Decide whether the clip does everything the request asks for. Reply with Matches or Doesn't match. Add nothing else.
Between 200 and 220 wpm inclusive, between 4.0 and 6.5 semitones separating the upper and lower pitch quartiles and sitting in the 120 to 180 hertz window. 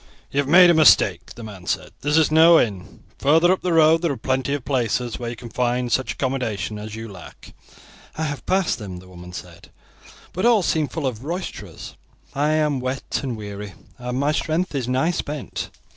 Matches